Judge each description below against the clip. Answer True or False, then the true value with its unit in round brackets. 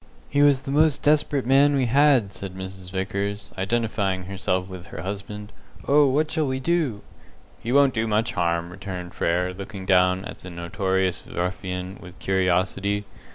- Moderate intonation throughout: False (5.9 semitones)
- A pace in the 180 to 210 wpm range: False (160 wpm)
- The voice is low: True (100 Hz)